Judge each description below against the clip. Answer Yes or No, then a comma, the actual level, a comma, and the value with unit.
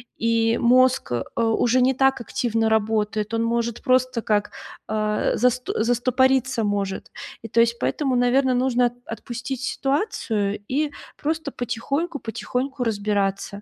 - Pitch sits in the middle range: No, high, 235 Hz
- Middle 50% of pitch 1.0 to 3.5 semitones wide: Yes, average, 2.8 semitones